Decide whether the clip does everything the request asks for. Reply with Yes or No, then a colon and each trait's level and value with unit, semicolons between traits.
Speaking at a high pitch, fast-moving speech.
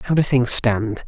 No: low, 120 Hz; fast, 225 wpm